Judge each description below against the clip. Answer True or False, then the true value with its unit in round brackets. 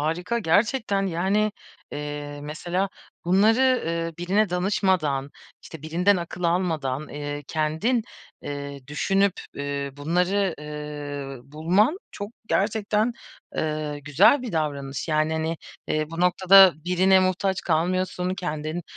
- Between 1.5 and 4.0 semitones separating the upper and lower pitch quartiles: False (4.5 semitones)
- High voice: False (170 Hz)